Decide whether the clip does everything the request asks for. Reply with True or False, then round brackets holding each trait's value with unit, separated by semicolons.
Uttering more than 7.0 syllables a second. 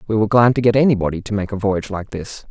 True (7.3 syllables/s)